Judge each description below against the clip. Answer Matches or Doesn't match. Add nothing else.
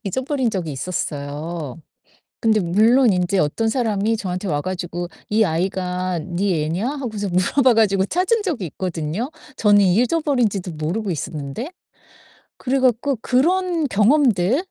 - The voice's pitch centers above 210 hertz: Doesn't match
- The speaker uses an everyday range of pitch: Doesn't match